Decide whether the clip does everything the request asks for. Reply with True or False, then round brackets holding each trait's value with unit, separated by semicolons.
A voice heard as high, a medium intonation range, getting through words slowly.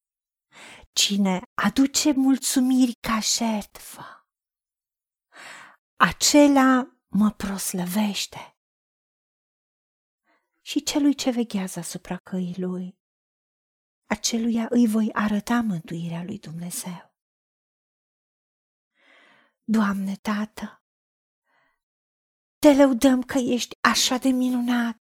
True (220 Hz; 4.7 semitones; 75 wpm)